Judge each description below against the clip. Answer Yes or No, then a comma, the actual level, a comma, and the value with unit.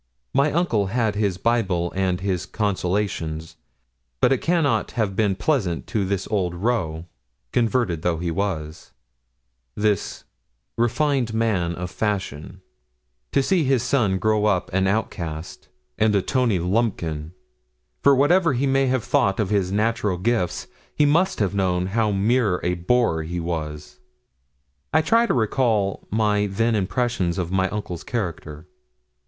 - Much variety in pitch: No, average, 4.9 semitones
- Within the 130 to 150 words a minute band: Yes, average, 145 wpm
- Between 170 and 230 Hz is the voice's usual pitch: No, low, 100 Hz